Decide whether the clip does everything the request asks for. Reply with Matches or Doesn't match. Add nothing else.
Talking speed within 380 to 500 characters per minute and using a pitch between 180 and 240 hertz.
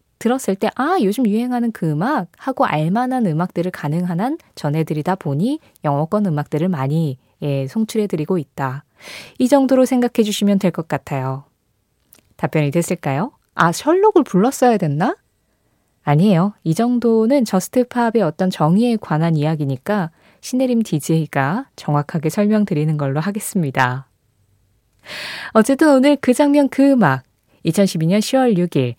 Doesn't match